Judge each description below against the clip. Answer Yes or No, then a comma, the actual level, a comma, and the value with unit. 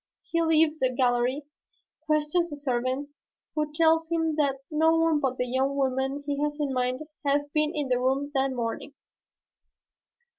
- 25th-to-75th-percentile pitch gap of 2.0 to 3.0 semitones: Yes, average, 2.7 semitones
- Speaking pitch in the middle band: No, very high, 285 Hz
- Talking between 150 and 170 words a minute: Yes, average, 160 wpm